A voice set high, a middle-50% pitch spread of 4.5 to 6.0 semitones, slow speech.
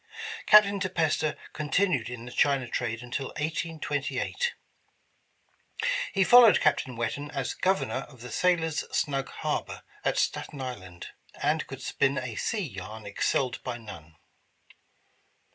No: low, 135 Hz; average, 5.1 semitones; slow, 130 wpm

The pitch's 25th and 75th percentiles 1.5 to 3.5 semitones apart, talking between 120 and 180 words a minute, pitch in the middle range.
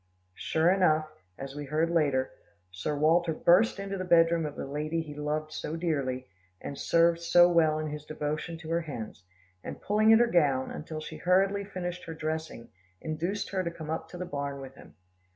No: average, 2.8 semitones; average, 200 wpm; medium, 160 Hz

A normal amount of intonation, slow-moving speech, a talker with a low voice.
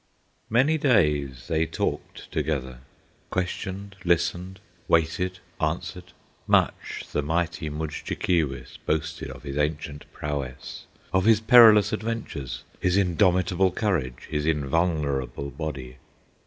Yes: average, 4.2 semitones; slow, 100 wpm; very low, 80 Hz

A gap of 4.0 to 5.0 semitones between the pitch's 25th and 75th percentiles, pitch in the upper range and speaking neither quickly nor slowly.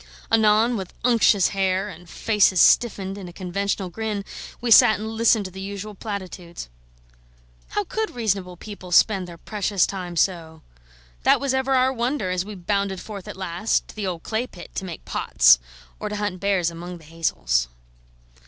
No: average, 3.3 semitones; high, 195 Hz; average, 175 wpm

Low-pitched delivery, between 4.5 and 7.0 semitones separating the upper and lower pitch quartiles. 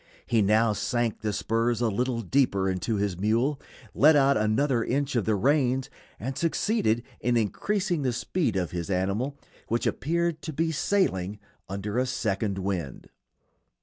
Yes: low, 115 Hz; wide, 5.4 semitones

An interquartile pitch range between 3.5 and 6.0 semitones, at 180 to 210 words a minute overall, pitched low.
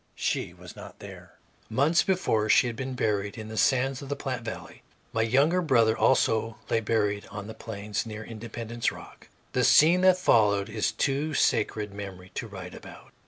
Yes: average, 3.9 semitones; average, 185 wpm; low, 115 Hz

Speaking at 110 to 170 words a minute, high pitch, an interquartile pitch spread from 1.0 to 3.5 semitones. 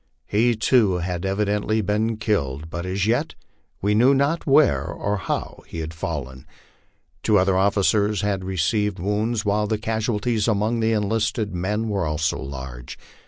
No: average, 155 wpm; low, 105 Hz; average, 3.2 semitones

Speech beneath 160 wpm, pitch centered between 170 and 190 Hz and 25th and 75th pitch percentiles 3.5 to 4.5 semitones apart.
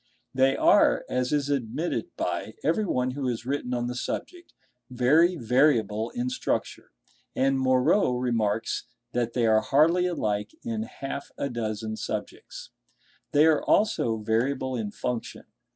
No: slow, 135 wpm; low, 125 Hz; average, 3.9 semitones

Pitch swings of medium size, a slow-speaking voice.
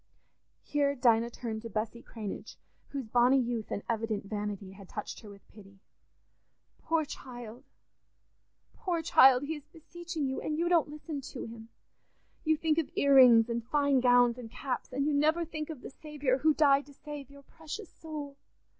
No: average, 4.6 semitones; average, 175 wpm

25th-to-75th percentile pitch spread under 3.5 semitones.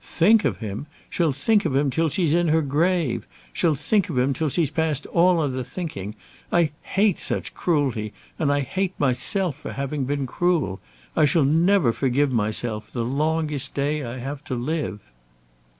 No: average, 4.3 semitones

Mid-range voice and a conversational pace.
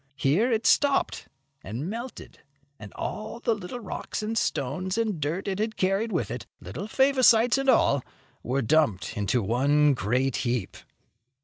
Yes: medium, 180 Hz; average, 145 wpm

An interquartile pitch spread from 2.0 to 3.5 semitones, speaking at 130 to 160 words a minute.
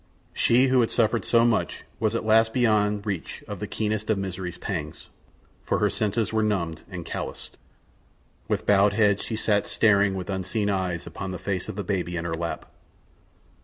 No: average, 2.9 semitones; average, 185 wpm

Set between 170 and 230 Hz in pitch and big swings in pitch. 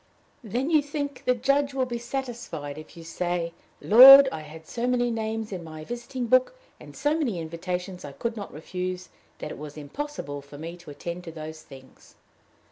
Yes: medium, 185 Hz; wide, 7.8 semitones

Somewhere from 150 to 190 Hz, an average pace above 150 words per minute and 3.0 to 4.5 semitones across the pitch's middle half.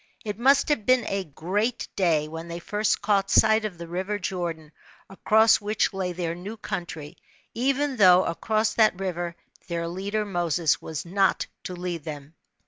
Yes: medium, 185 Hz; average, 165 wpm; average, 4.0 semitones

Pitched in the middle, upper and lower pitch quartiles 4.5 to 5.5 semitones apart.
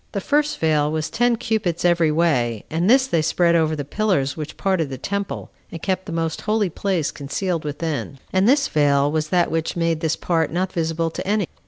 No: medium, 165 Hz; average, 3.7 semitones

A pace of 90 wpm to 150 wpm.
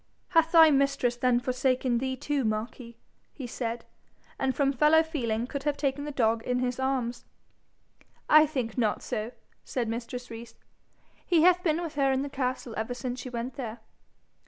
No: average, 175 wpm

